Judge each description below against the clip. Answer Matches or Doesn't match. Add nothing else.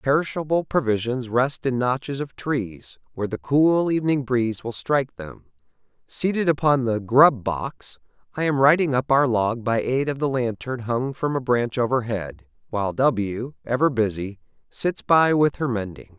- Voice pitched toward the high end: Doesn't match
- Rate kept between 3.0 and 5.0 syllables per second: Matches